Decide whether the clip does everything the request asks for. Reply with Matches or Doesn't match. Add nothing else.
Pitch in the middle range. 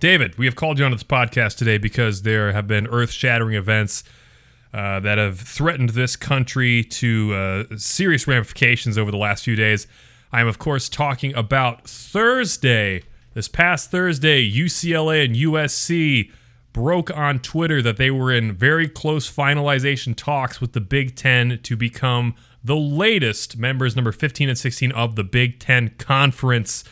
Doesn't match